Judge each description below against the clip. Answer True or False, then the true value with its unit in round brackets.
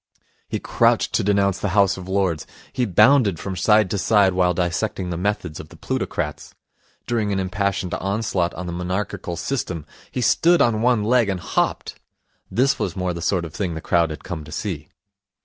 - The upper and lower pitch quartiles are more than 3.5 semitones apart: False (3.2 semitones)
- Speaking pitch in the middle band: False (95 Hz)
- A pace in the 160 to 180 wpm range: False (190 wpm)